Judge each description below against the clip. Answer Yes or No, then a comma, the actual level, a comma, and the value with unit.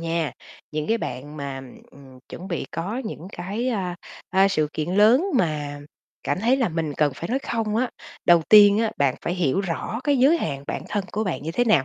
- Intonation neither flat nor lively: No, wide, 6.4 semitones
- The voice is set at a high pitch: No, medium, 180 Hz